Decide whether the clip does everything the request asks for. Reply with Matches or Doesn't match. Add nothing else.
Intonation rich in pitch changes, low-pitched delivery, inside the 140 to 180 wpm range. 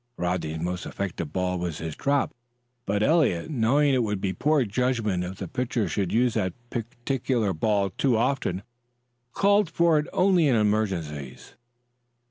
Matches